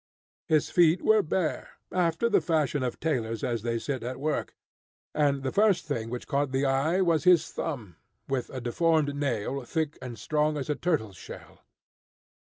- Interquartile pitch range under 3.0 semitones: No, average, 4.2 semitones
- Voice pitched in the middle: Yes, medium, 145 Hz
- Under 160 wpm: No, average, 175 wpm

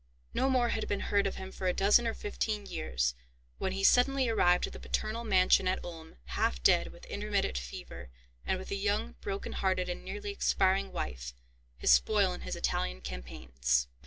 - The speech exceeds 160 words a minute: Yes, average, 190 wpm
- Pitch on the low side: No, high, 190 Hz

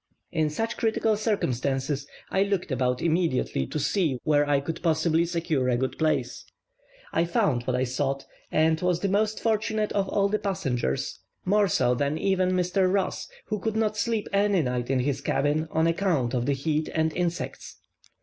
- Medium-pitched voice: Yes, medium, 160 Hz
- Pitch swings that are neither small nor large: No, wide, 6.2 semitones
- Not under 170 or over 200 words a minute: Yes, average, 180 wpm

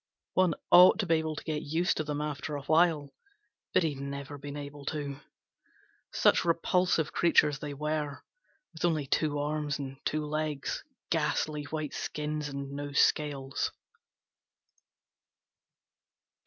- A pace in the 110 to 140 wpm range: Yes, slow, 135 wpm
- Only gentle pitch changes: Yes, narrow, 1.6 semitones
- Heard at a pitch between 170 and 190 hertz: No, medium, 150 Hz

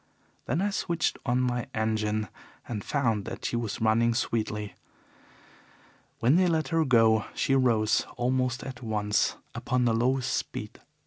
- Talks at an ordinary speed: Yes, average, 145 wpm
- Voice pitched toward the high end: No, low, 120 Hz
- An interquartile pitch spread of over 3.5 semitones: No, average, 2.9 semitones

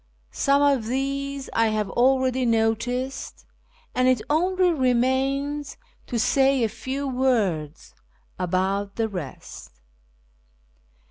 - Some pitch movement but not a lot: Yes, average, 3.7 semitones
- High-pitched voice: Yes, very high, 255 Hz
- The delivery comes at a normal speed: No, slow, 105 wpm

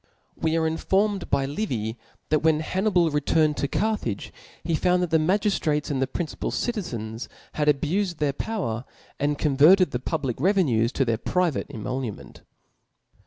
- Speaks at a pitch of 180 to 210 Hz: No, medium, 155 Hz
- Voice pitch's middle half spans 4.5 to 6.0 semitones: Yes, average, 5.2 semitones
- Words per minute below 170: Yes, average, 145 wpm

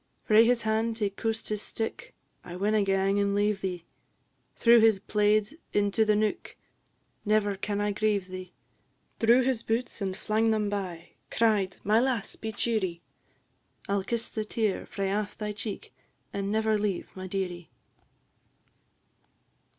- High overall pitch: Yes, high, 210 Hz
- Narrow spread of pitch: Yes, narrow, 2.1 semitones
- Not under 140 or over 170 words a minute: Yes, average, 150 wpm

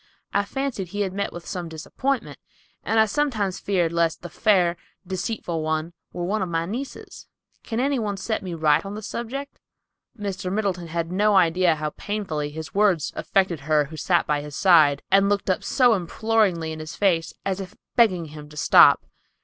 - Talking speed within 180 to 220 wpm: Yes, average, 190 wpm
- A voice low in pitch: No, medium, 185 Hz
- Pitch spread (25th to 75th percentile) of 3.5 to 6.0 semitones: Yes, average, 4.1 semitones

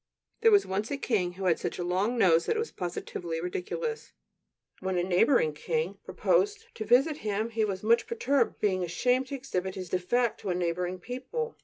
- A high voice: Yes, high, 210 Hz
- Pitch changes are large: Yes, wide, 7.1 semitones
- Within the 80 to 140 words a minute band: No, average, 195 wpm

